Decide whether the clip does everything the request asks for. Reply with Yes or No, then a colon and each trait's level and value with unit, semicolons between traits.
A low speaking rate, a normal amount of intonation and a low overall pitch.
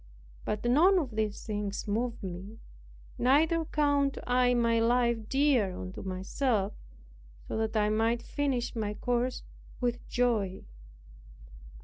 No: slow, 120 wpm; average, 3.3 semitones; high, 235 Hz